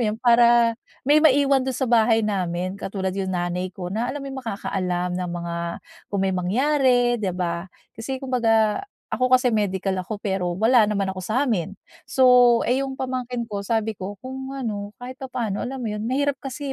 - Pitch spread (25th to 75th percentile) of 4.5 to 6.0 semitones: Yes, average, 5.1 semitones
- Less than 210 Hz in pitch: No, high, 225 Hz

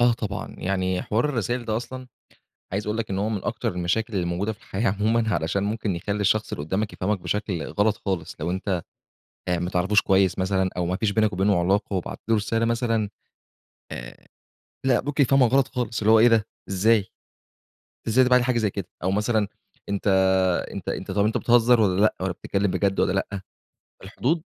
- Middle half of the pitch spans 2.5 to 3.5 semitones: Yes, average, 3.2 semitones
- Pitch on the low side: Yes, low, 105 Hz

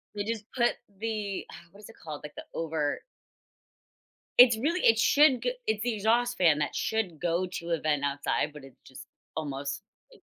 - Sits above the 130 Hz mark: Yes, high, 190 Hz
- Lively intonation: Yes, wide, 7.0 semitones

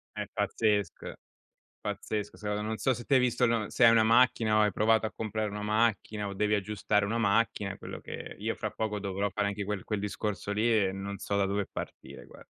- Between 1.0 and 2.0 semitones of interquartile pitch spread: Yes, narrow, 1.6 semitones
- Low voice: Yes, low, 105 Hz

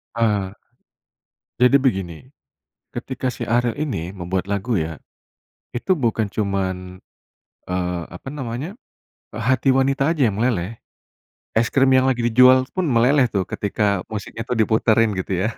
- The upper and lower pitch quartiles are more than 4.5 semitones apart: Yes, average, 5.0 semitones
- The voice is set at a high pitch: No, low, 115 Hz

